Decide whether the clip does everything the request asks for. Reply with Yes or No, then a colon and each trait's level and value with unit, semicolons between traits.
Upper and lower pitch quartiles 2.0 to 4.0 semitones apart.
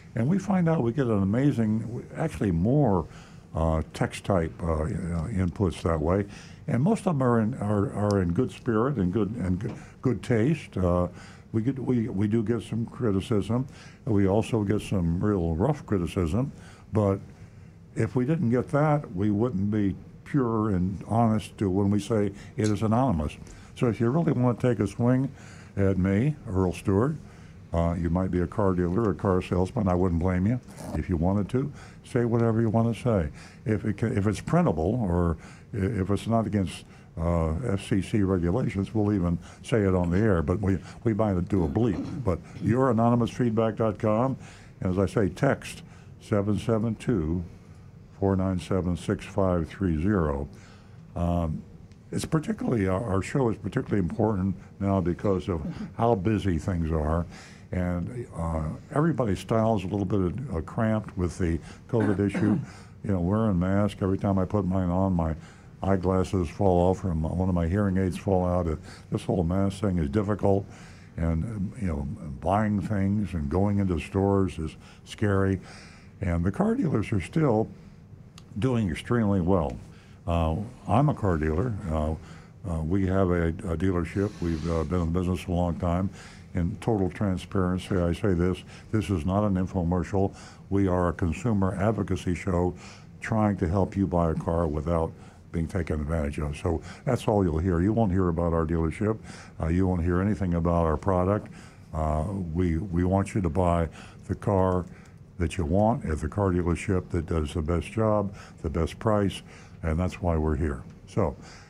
Yes: average, 3.6 semitones